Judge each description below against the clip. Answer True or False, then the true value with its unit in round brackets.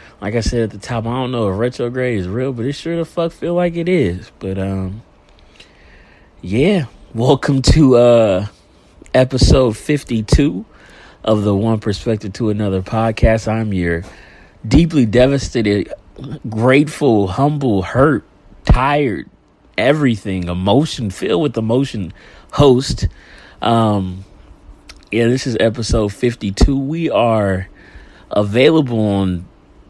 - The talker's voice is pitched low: True (115 Hz)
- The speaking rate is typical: False (125 wpm)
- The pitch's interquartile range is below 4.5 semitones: False (4.8 semitones)